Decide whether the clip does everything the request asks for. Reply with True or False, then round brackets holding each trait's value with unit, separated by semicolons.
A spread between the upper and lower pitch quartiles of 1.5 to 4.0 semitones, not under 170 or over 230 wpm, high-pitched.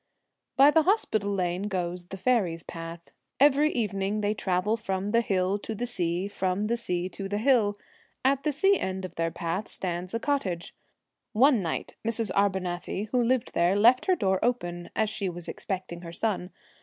False (4.5 semitones; 190 wpm; 200 Hz)